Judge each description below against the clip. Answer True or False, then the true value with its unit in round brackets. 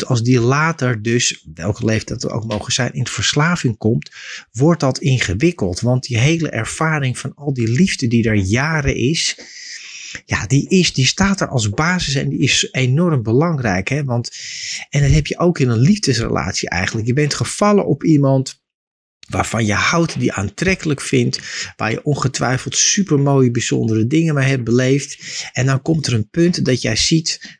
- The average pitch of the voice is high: False (130 Hz)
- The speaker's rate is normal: True (180 wpm)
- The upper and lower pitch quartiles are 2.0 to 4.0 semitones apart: False (4.7 semitones)